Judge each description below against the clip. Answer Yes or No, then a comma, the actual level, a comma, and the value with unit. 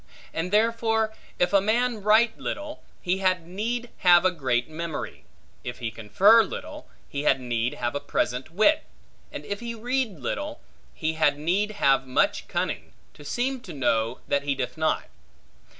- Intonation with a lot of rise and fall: Yes, wide, 8.3 semitones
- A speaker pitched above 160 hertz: Yes, medium, 185 Hz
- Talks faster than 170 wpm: No, average, 165 wpm